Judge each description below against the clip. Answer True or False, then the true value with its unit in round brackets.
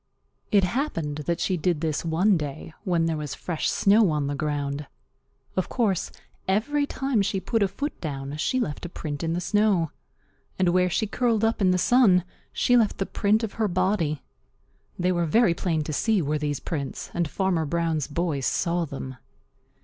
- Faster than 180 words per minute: True (190 wpm)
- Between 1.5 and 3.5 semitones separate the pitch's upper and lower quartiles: False (5.2 semitones)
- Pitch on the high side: False (175 Hz)